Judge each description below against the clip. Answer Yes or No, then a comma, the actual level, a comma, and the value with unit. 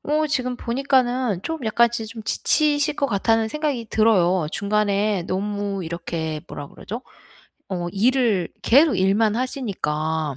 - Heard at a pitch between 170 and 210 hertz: No, high, 220 Hz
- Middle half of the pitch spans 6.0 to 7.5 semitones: No, average, 5.2 semitones